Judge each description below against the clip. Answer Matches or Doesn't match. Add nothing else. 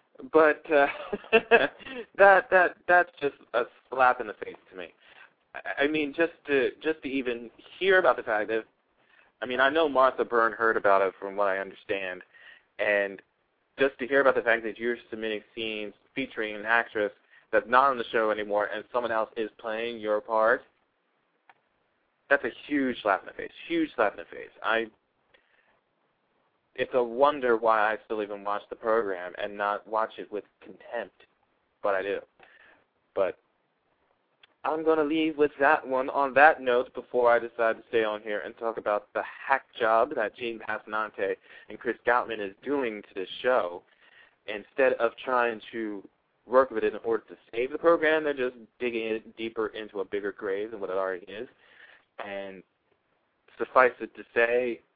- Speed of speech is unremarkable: Matches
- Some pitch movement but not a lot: Doesn't match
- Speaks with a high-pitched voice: Doesn't match